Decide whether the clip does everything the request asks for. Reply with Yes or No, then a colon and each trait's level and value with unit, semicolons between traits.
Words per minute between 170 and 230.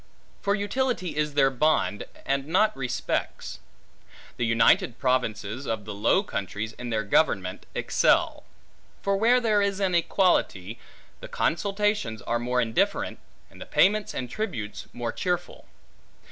No: slow, 135 wpm